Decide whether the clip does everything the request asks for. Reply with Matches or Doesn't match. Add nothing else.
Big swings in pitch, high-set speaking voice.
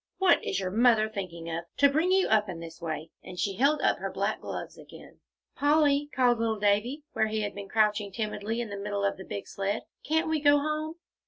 Matches